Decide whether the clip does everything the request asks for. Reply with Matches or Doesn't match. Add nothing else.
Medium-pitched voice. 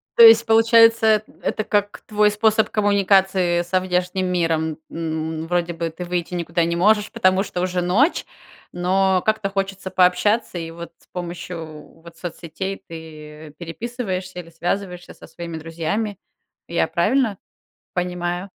Matches